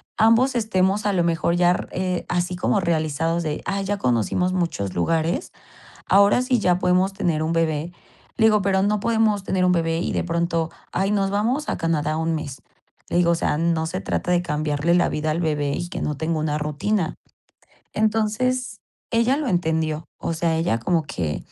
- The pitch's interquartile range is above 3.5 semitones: Yes, average, 4.0 semitones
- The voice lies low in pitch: No, medium, 175 Hz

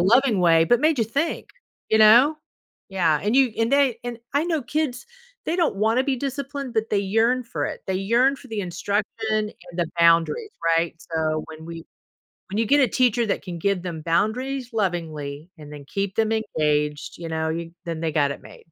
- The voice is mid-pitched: No, high, 210 Hz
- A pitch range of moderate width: No, wide, 7.1 semitones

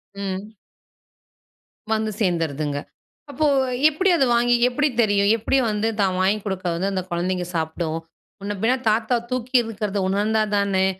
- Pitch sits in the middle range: No, high, 200 Hz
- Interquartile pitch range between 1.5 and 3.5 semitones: Yes, average, 3.2 semitones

